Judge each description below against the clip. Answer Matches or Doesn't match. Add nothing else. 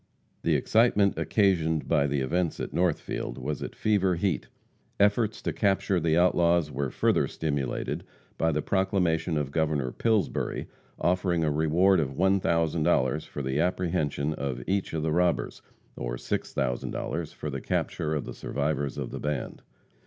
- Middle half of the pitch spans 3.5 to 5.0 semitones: Matches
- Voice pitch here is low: Matches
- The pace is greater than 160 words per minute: Doesn't match